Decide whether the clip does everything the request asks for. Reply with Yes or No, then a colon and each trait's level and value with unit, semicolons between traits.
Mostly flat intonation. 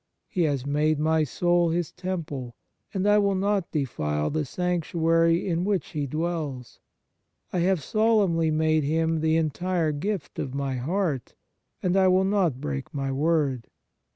No: average, 4.0 semitones